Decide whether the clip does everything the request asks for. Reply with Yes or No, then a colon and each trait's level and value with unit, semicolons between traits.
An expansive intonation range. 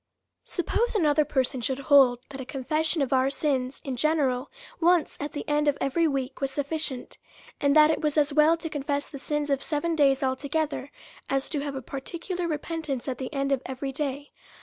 No: narrow, 2.4 semitones